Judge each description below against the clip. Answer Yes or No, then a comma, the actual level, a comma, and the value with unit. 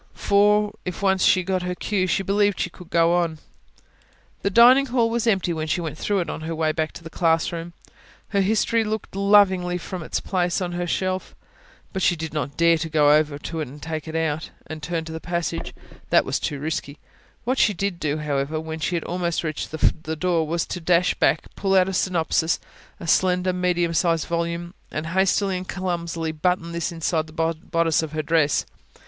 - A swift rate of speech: Yes, fast, 210 wpm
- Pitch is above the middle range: No, medium, 170 Hz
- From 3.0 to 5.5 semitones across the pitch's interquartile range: No, narrow, 2.6 semitones